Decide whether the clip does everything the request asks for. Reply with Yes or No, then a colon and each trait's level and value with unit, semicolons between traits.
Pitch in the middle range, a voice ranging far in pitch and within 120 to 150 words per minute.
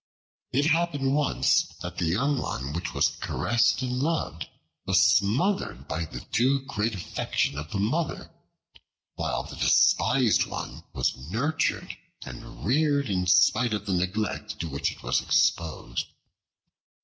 No: low, 110 Hz; wide, 7.5 semitones; average, 140 wpm